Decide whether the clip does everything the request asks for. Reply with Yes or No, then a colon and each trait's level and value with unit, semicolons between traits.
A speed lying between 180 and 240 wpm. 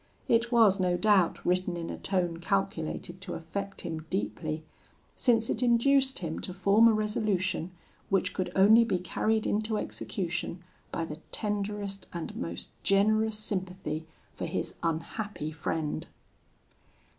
No: slow, 135 wpm